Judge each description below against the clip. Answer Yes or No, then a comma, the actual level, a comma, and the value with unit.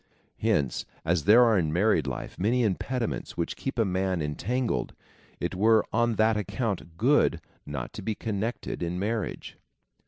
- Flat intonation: No, average, 4.9 semitones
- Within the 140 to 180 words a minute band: Yes, average, 160 wpm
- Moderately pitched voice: No, low, 105 Hz